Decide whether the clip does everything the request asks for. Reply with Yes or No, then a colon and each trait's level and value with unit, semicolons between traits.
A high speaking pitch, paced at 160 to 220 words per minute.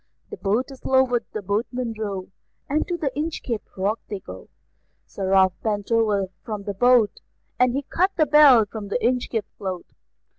Yes: high, 225 Hz; average, 175 wpm